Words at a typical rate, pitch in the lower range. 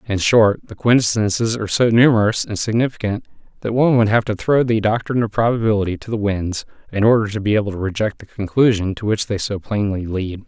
No: fast, 210 wpm; low, 105 Hz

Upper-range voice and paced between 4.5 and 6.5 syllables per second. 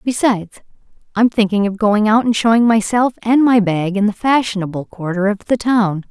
Yes: high, 215 Hz; 5.2 syllables/s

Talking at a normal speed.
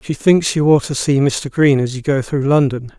No: fast, 260 wpm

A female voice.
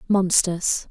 Yes: female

